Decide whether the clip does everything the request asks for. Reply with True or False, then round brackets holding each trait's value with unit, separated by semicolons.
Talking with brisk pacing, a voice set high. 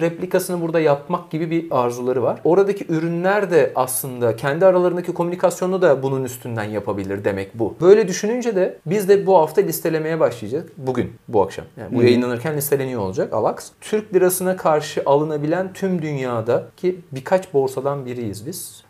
False (150 wpm; 160 Hz)